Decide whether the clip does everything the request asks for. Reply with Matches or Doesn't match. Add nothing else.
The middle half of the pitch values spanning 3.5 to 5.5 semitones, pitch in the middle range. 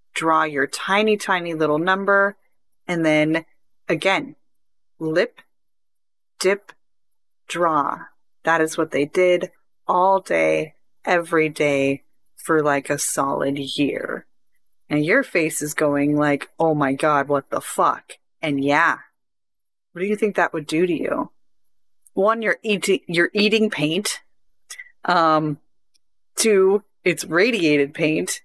Matches